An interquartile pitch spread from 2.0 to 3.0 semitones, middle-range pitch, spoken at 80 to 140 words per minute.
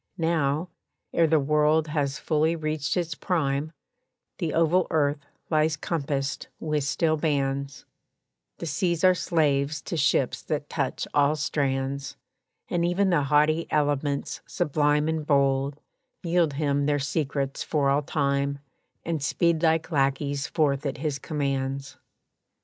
Yes: narrow, 2.4 semitones; medium, 150 Hz; slow, 135 wpm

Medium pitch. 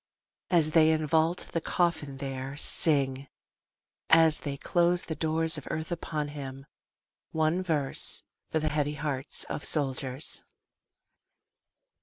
Yes: medium, 155 Hz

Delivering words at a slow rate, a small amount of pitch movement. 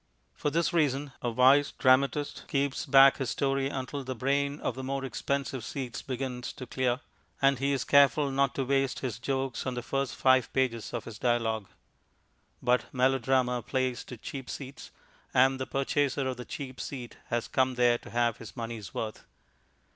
No: average, 175 wpm; narrow, 1.9 semitones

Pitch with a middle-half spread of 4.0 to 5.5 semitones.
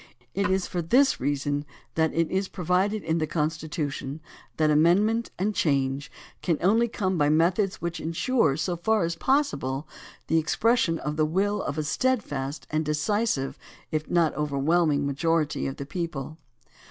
Yes: average, 4.3 semitones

